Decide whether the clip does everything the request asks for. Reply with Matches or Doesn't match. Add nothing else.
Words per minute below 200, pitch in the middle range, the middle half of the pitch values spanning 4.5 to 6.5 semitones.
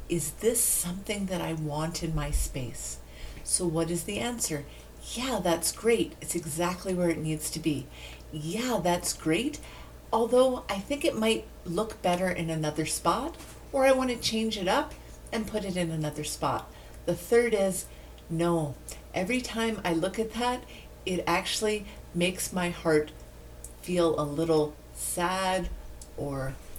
Matches